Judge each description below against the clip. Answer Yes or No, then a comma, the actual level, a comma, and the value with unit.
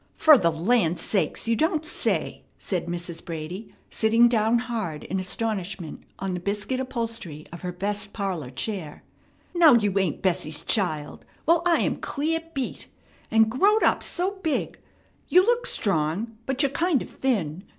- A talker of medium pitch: No, high, 210 Hz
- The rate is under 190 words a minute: Yes, average, 160 wpm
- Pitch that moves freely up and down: Yes, wide, 7.0 semitones